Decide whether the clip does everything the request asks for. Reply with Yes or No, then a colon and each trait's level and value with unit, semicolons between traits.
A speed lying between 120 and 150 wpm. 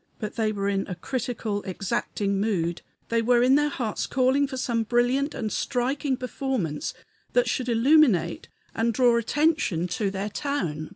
No: average, 160 wpm